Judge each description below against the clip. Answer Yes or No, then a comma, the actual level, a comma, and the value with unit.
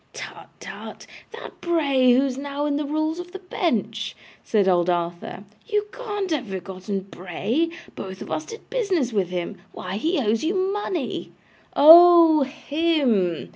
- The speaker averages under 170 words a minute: Yes, average, 155 wpm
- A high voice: Yes, very high, 285 Hz